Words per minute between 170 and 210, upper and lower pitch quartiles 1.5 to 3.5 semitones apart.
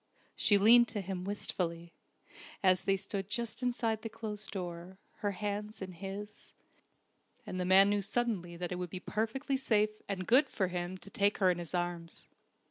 Yes: average, 180 wpm; average, 2.9 semitones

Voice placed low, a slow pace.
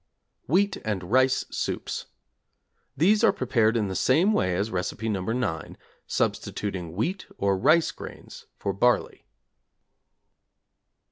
Yes: low, 110 Hz; slow, 120 wpm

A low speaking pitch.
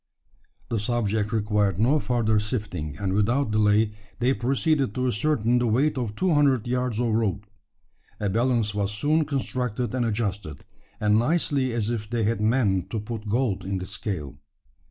Yes: low, 110 Hz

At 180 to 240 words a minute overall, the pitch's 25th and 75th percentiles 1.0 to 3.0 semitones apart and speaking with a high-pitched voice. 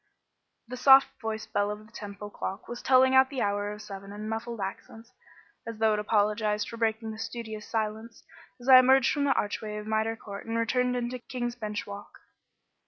Yes: average, 195 wpm; narrow, 2.4 semitones; high, 220 Hz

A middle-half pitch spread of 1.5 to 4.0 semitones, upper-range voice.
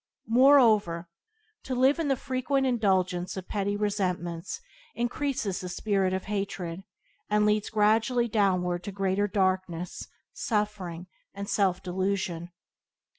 Yes: average, 3.2 semitones; high, 200 Hz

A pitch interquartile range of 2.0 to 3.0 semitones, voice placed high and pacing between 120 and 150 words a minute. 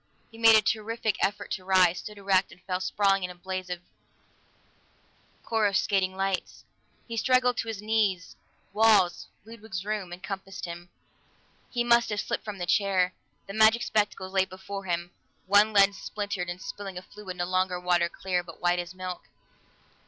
No: narrow, 2.6 semitones; high, 195 Hz; average, 165 wpm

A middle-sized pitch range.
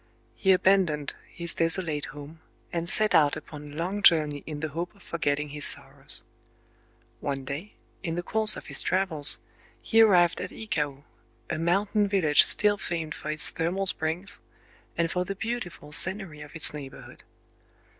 Yes: average, 4.4 semitones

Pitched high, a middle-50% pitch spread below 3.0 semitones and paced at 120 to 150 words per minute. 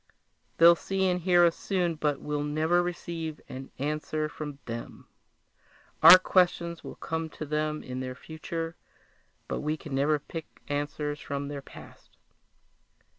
No: medium, 155 Hz; narrow, 2.6 semitones; average, 145 wpm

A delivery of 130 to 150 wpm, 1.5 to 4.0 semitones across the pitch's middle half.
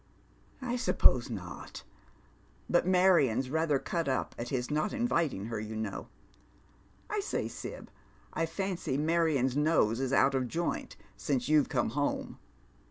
No: average, 145 wpm; wide, 5.5 semitones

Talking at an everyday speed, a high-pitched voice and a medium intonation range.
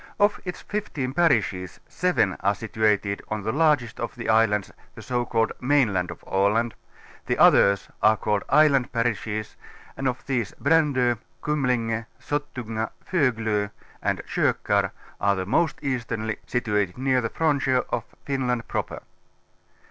No: average, 150 wpm; low, 120 Hz; average, 4.1 semitones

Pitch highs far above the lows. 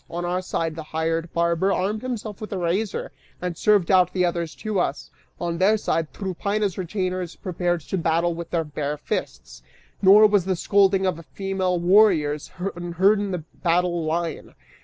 No: narrow, 2.6 semitones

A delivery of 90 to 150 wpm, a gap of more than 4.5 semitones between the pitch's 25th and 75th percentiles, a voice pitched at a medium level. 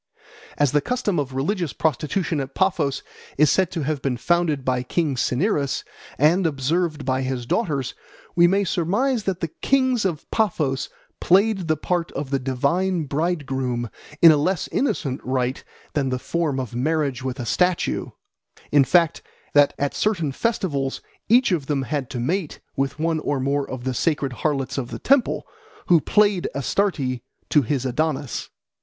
No: average, 165 wpm; average, 4.9 semitones; medium, 150 Hz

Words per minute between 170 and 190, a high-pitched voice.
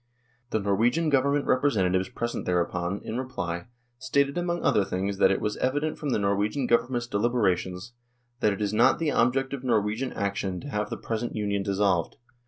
No: average, 180 wpm; low, 110 Hz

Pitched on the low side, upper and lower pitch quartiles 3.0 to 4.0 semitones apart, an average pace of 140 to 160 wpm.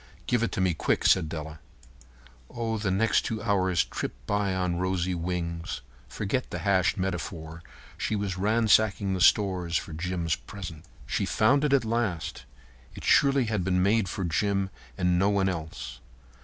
No: very low, 95 Hz; average, 3.5 semitones; average, 170 wpm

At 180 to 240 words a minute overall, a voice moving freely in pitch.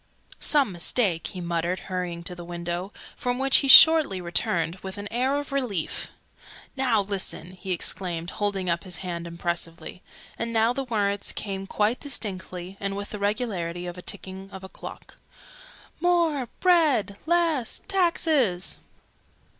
No: average, 145 wpm; wide, 5.9 semitones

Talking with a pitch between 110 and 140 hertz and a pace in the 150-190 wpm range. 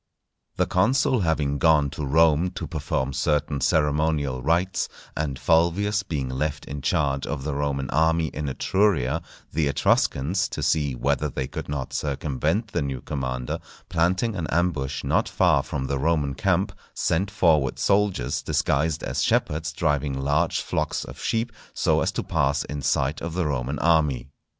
No: very low, 75 Hz; average, 160 wpm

